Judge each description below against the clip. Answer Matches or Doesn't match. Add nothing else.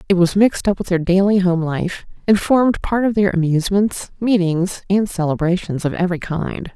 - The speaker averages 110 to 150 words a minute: Doesn't match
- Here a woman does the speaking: Matches